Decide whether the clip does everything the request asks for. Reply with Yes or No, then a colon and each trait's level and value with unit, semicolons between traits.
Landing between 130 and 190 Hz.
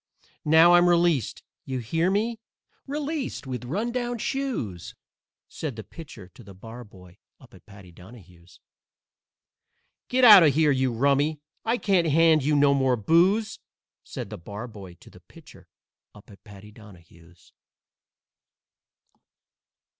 Yes: low, 135 Hz